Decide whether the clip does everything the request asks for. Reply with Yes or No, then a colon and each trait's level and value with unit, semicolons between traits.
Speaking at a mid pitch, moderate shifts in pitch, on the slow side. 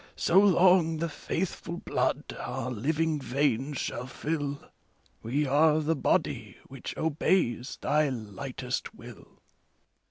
Yes: medium, 150 Hz; average, 3.9 semitones; slow, 115 wpm